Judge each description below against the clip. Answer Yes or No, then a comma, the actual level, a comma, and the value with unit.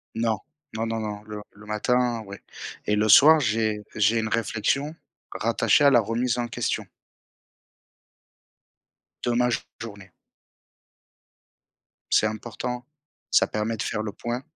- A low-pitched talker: Yes, low, 115 Hz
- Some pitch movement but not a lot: No, narrow, 2.3 semitones